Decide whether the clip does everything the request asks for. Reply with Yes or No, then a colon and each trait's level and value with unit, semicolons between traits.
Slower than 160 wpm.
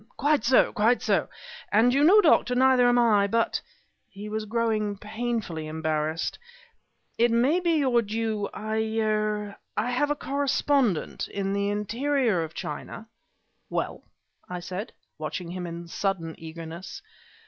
Yes: average, 145 wpm